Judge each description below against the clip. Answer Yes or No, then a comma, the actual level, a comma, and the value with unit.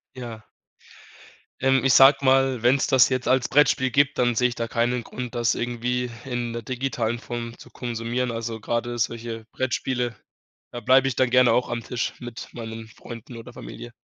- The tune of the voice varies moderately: No, narrow, 1.7 semitones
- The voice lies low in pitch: Yes, low, 120 Hz